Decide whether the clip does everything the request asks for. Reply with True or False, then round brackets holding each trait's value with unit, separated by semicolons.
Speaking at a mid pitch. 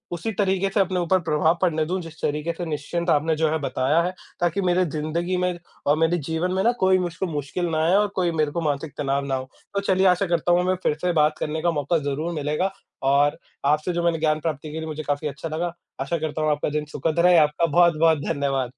True (160 Hz)